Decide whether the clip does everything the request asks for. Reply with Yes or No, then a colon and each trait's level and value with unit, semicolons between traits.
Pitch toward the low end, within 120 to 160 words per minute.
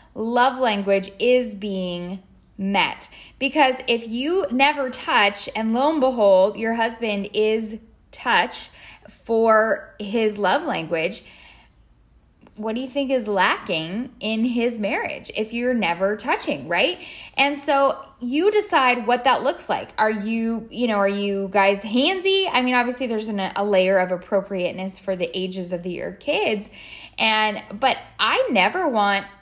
No: high, 220 Hz; average, 145 wpm